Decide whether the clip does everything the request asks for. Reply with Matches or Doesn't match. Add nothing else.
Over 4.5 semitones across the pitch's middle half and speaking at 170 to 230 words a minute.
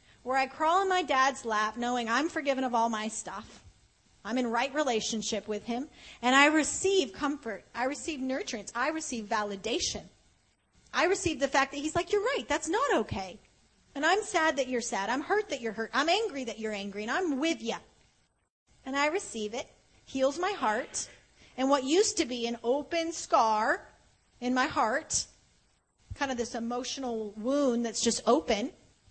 Matches